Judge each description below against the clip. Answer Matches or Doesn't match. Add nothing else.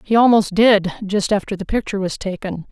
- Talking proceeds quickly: Doesn't match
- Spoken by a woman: Matches